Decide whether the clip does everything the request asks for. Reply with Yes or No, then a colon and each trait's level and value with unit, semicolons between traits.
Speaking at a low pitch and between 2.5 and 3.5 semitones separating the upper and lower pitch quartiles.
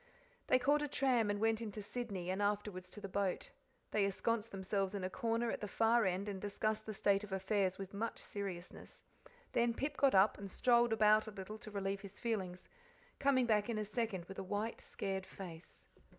No: high, 205 Hz; average, 2.8 semitones